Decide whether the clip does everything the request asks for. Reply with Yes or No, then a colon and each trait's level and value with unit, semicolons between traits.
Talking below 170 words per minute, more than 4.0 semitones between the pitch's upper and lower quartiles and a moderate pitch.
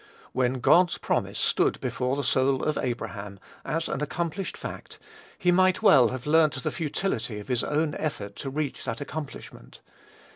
Yes: average, 160 wpm; average, 4.4 semitones; medium, 145 Hz